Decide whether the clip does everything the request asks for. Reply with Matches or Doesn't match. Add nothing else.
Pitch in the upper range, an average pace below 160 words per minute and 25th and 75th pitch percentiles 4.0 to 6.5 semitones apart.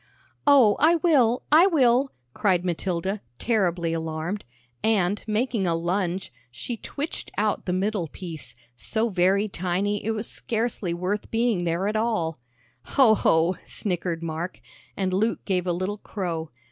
Matches